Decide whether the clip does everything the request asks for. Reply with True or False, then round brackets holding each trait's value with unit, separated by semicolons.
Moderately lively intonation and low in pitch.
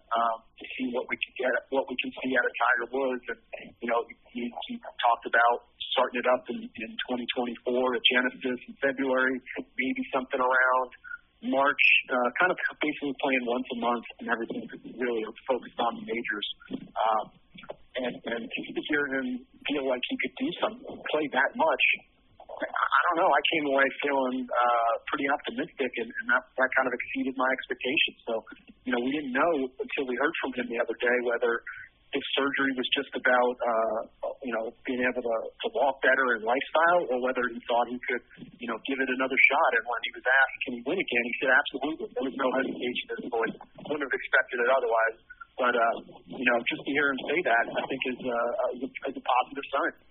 True (3.2 semitones; 130 Hz)